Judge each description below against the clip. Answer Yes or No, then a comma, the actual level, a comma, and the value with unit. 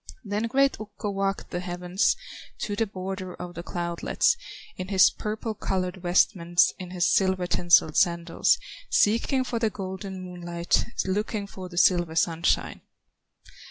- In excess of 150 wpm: No, average, 140 wpm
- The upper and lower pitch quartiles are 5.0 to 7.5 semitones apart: No, narrow, 2.6 semitones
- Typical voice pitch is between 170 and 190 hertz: Yes, medium, 185 Hz